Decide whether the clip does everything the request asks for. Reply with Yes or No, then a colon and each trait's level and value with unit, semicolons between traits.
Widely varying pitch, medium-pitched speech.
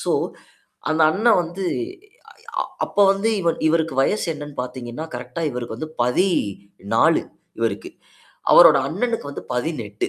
Yes: wide, 6.0 semitones; medium, 155 Hz